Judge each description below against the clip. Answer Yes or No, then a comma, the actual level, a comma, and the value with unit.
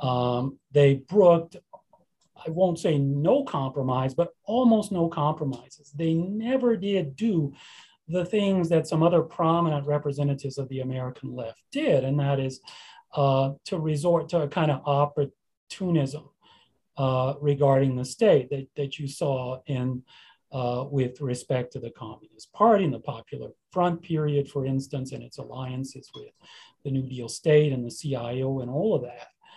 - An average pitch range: Yes, average, 4.0 semitones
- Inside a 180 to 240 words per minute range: No, average, 155 wpm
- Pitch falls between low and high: Yes, medium, 145 Hz